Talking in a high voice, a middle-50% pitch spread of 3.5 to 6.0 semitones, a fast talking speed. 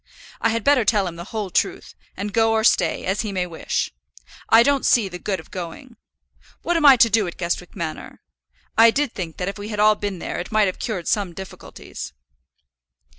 Yes: high, 205 Hz; average, 3.9 semitones; fast, 215 wpm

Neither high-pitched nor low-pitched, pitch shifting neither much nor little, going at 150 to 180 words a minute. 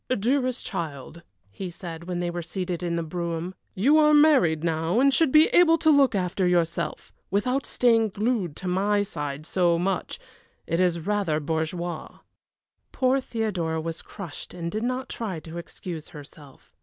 No: medium, 180 Hz; wide, 5.7 semitones; average, 165 wpm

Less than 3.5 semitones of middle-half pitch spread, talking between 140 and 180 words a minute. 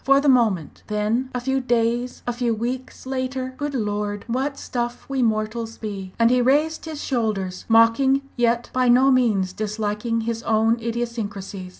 Yes: average, 3.1 semitones; average, 165 wpm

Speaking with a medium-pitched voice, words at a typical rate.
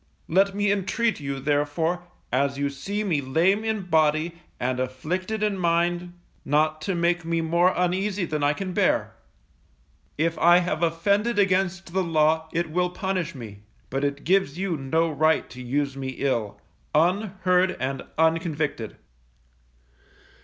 Yes: medium, 165 Hz; average, 145 wpm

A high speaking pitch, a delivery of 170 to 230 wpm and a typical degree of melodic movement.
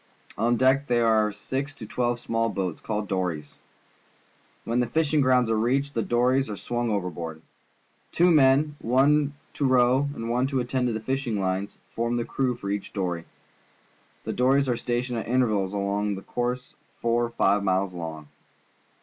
No: low, 120 Hz; average, 175 wpm; average, 4.3 semitones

